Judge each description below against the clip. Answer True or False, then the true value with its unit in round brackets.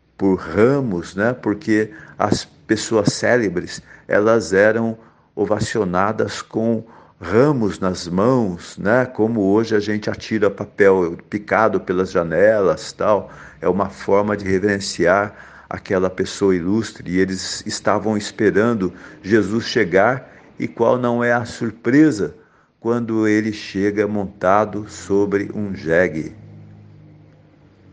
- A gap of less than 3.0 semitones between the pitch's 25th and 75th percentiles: True (2.5 semitones)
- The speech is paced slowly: True (110 wpm)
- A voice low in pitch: True (105 Hz)